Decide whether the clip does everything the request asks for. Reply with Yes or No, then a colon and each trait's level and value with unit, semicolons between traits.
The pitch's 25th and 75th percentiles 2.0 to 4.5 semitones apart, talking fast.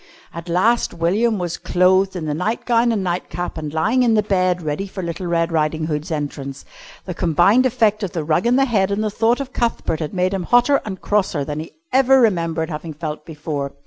No: average, 5.2 semitones; fast, 210 wpm